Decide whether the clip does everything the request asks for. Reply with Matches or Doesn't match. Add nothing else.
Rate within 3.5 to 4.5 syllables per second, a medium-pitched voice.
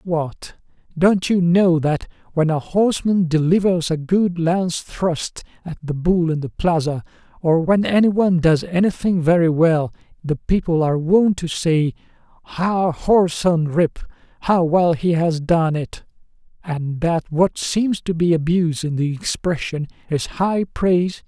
Matches